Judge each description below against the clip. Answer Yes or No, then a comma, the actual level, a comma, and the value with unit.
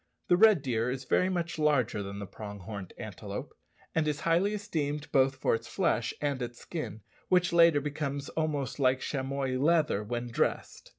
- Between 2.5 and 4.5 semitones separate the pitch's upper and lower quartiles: No, average, 5.0 semitones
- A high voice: No, medium, 140 Hz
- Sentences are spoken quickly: No, average, 175 wpm